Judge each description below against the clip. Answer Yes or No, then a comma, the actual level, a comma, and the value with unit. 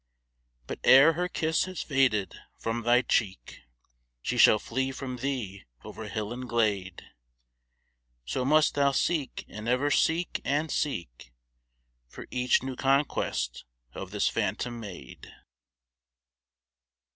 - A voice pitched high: No, low, 125 Hz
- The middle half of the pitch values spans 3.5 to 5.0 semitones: Yes, average, 4.7 semitones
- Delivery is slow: Yes, slow, 120 wpm